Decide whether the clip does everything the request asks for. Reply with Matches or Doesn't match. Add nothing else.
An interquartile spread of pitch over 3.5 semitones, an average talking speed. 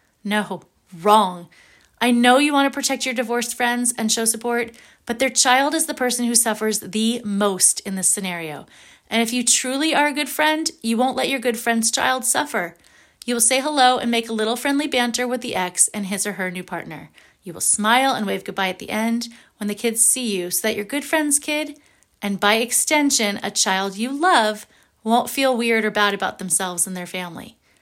Doesn't match